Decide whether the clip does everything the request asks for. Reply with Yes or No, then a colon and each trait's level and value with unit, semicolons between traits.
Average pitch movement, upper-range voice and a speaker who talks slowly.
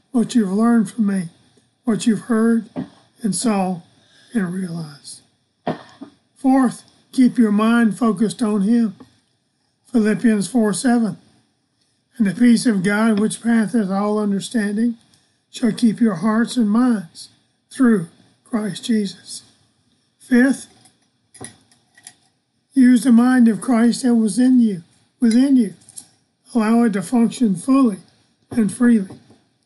Yes: average, 3.4 semitones; high, 225 Hz; slow, 120 wpm